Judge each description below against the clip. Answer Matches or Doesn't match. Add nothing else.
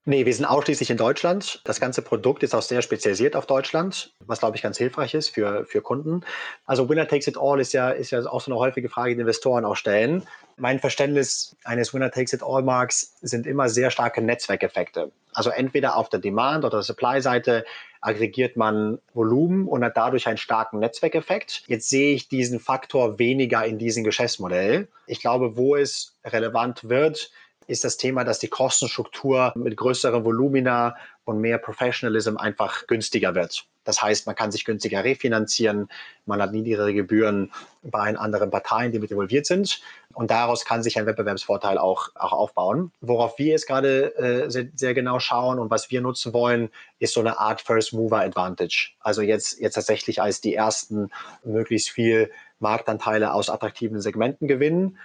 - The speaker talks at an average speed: Matches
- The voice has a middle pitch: Doesn't match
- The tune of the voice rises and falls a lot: Doesn't match